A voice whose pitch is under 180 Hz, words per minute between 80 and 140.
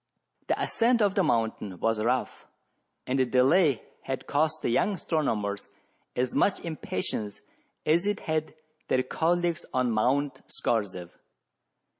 Yes: low, 135 Hz; slow, 135 wpm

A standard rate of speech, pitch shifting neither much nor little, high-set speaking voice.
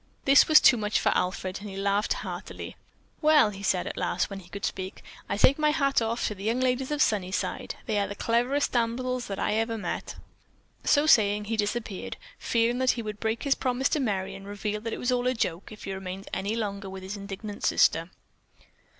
No: fast, 220 wpm; average, 3.8 semitones; high, 215 Hz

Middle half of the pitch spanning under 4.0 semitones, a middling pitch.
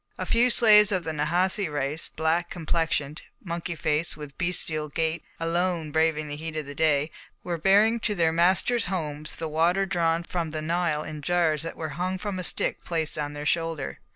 Yes: narrow, 2.6 semitones; medium, 165 Hz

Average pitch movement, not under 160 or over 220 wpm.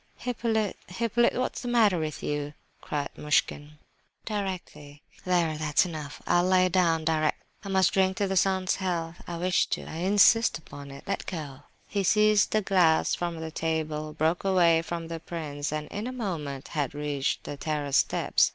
Yes: average, 4.0 semitones; average, 175 wpm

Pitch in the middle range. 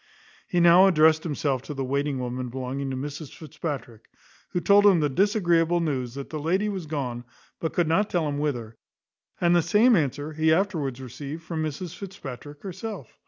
Yes: medium, 155 Hz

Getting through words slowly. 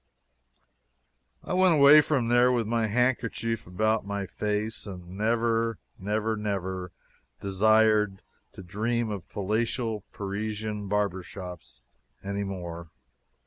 Yes: slow, 105 wpm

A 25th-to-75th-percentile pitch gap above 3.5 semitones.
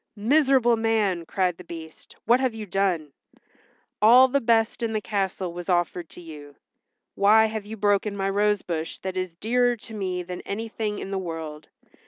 Yes: average, 4.0 semitones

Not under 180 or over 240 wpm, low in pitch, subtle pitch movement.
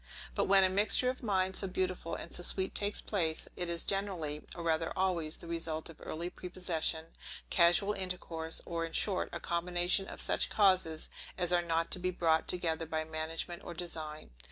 No: average, 185 wpm; medium, 175 Hz; narrow, 2.3 semitones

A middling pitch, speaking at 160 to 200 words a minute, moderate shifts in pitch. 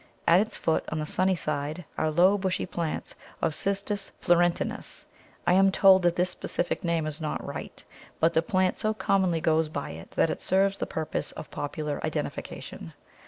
Yes: medium, 175 Hz; average, 180 wpm; average, 3.3 semitones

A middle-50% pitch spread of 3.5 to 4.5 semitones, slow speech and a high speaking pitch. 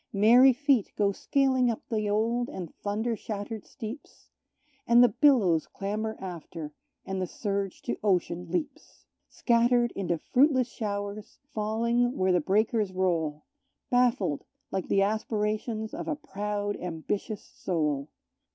Yes: average, 4.0 semitones; slow, 130 wpm; high, 210 Hz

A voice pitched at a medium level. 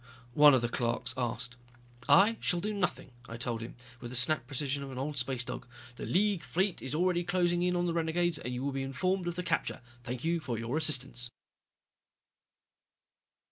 Yes: medium, 145 Hz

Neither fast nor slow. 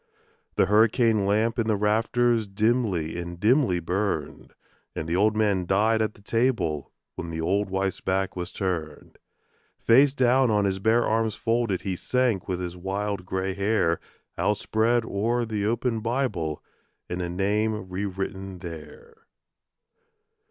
Yes: average, 145 wpm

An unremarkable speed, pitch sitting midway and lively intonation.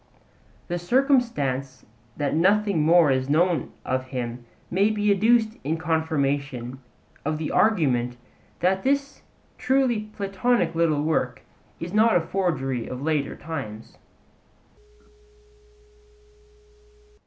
No: slow, 105 wpm; medium, 165 Hz; wide, 7.1 semitones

